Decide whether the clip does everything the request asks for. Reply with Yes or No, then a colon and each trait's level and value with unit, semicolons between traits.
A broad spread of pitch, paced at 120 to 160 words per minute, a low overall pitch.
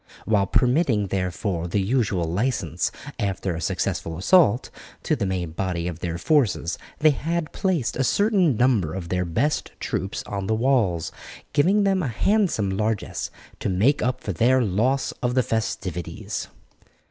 Yes: wide, 6.7 semitones; average, 155 wpm; low, 110 Hz